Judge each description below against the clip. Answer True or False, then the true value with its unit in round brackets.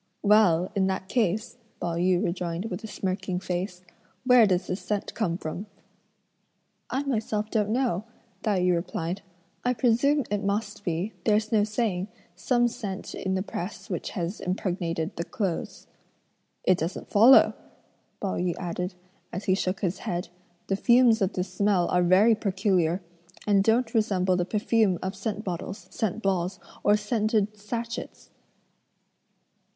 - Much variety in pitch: False (3.1 semitones)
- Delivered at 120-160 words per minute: True (150 wpm)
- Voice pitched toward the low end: False (195 Hz)